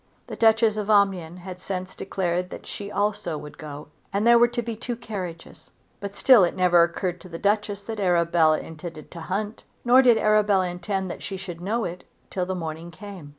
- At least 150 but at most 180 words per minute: No, average, 200 wpm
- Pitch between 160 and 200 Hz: Yes, high, 190 Hz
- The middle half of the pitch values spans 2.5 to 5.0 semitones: Yes, average, 3.5 semitones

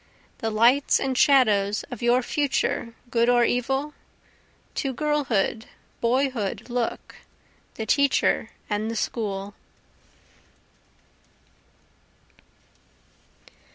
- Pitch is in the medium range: No, high, 240 Hz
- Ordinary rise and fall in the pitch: Yes, average, 3.4 semitones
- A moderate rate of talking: No, slow, 85 wpm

